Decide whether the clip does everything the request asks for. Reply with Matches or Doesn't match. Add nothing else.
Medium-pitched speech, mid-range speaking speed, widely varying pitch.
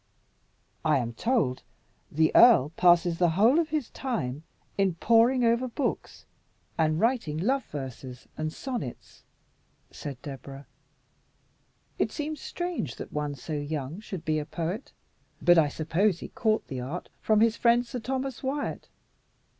Matches